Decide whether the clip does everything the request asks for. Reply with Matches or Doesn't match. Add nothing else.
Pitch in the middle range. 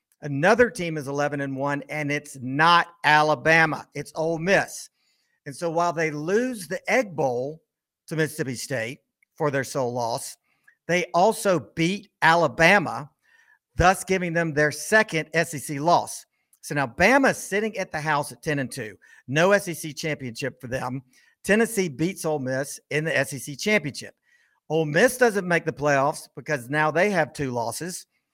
Matches